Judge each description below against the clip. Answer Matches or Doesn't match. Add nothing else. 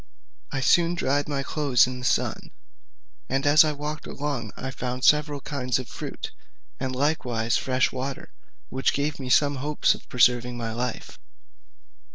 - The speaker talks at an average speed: Matches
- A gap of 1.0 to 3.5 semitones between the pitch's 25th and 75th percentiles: Matches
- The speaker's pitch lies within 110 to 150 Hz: Matches